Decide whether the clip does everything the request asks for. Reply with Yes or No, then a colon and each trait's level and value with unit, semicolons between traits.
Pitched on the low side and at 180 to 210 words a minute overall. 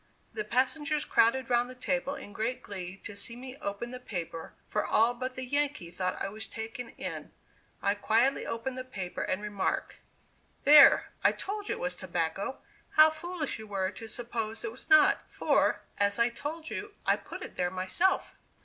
No: high, 235 Hz; average, 185 wpm